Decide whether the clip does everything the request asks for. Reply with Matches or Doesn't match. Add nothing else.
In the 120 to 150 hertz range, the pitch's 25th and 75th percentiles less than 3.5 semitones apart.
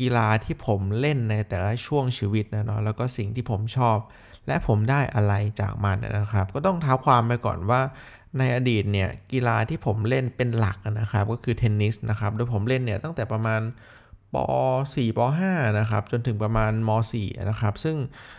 Doesn't match